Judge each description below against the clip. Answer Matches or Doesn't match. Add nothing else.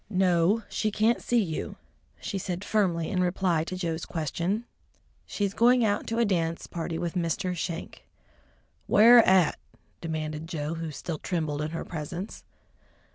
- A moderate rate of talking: Matches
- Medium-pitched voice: Matches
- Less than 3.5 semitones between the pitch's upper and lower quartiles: Doesn't match